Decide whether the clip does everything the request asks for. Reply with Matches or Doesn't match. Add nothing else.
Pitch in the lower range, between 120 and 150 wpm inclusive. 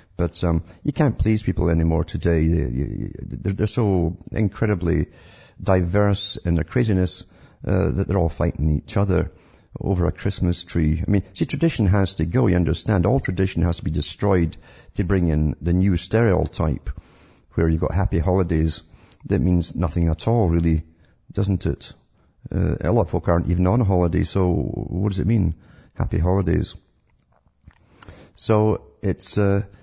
Doesn't match